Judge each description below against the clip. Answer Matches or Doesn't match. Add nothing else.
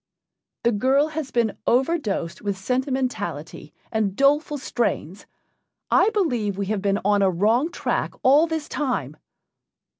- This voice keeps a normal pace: Doesn't match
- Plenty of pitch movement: Matches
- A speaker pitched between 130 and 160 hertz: Doesn't match